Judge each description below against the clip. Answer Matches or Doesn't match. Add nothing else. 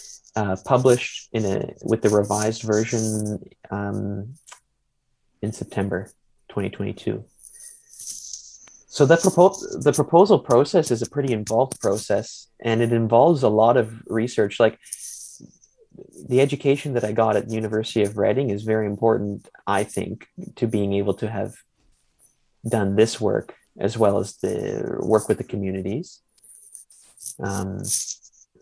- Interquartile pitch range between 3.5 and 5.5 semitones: Doesn't match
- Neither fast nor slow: Doesn't match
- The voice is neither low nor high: Doesn't match